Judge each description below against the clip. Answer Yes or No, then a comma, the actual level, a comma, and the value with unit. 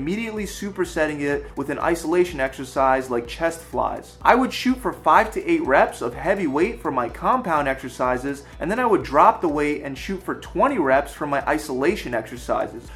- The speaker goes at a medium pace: Yes, average, 195 wpm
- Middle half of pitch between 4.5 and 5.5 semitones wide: Yes, average, 4.8 semitones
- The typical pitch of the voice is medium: Yes, medium, 150 Hz